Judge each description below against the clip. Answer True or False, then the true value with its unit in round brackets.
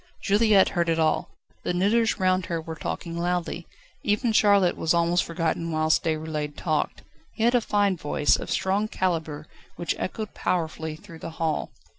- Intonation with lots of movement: False (3.7 semitones)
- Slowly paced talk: False (165 wpm)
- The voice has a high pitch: False (170 Hz)